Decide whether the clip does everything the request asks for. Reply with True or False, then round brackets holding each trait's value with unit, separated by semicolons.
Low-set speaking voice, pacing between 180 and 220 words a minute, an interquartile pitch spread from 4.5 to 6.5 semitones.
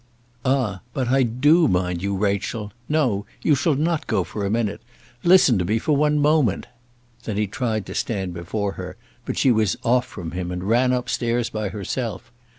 True (115 Hz; 190 wpm; 4.9 semitones)